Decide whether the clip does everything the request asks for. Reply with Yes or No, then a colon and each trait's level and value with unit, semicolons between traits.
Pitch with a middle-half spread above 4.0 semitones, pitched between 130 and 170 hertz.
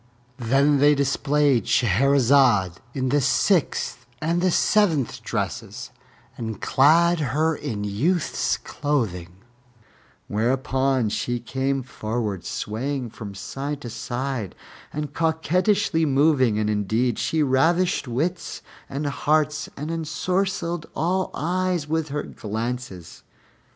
Yes: average, 5.1 semitones; medium, 140 Hz